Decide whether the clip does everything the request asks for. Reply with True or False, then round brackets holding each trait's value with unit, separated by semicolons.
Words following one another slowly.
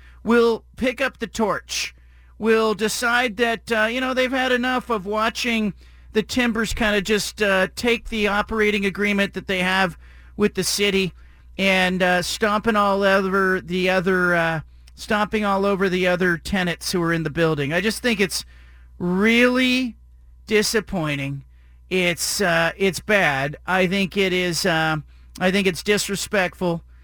False (155 wpm)